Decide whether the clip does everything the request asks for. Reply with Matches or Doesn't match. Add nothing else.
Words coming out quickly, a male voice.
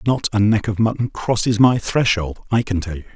Matches